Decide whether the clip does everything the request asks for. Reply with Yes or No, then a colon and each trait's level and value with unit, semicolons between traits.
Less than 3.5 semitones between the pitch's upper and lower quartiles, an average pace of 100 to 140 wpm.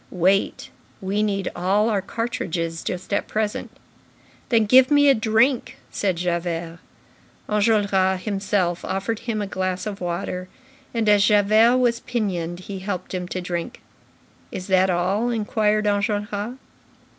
Yes: average, 2.9 semitones; slow, 135 wpm